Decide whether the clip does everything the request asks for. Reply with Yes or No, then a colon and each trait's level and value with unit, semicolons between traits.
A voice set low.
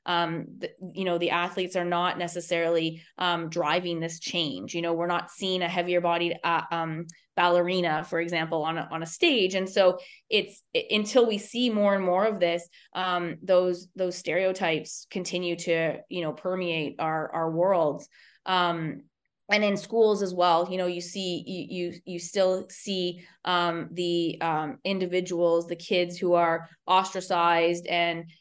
No: medium, 175 Hz